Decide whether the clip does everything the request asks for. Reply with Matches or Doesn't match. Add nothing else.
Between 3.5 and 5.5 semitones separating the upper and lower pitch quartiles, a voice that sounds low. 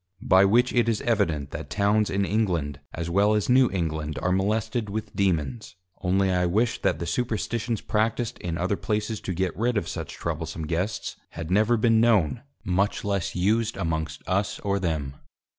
Matches